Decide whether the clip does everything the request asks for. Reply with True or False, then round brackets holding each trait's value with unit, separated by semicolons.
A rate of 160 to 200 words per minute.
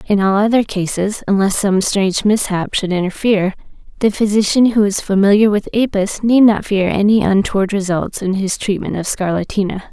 True (170 wpm)